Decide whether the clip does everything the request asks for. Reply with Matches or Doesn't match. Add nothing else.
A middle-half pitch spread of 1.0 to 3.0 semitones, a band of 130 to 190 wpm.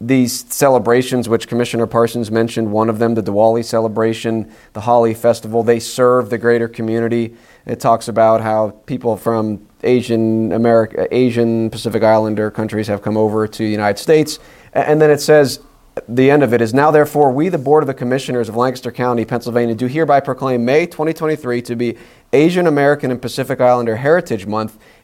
Matches